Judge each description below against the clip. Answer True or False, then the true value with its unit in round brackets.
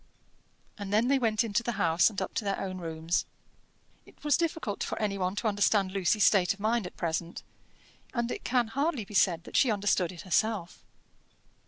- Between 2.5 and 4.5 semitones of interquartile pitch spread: True (3.7 semitones)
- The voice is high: True (205 Hz)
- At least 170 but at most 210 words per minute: True (195 wpm)